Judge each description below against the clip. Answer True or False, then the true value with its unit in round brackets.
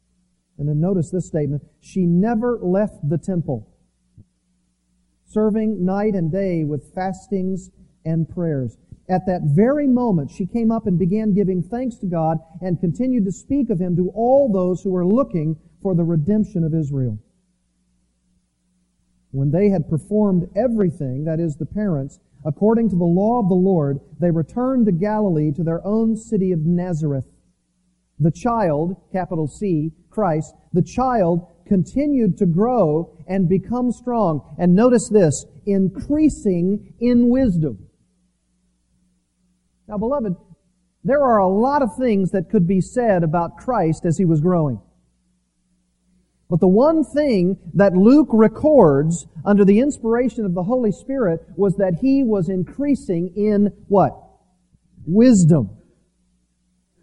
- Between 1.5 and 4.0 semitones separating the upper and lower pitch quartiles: False (5.4 semitones)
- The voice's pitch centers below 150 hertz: False (180 Hz)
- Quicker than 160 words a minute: False (140 wpm)